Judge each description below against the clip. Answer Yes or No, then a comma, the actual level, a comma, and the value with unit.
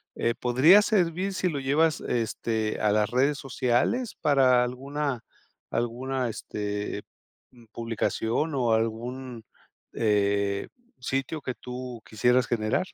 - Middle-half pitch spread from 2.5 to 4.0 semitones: Yes, average, 3.6 semitones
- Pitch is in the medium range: No, low, 125 Hz